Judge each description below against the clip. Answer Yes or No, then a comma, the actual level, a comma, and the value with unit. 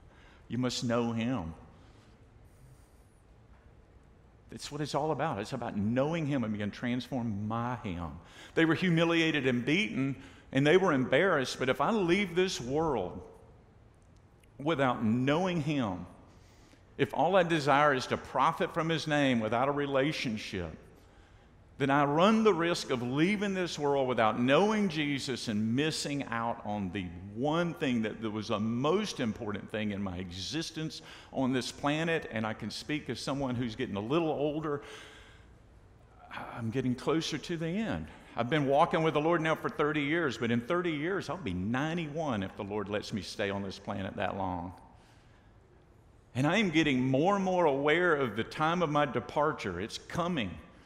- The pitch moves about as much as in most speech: No, wide, 6.1 semitones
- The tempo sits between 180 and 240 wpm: No, average, 165 wpm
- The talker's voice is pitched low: Yes, low, 125 Hz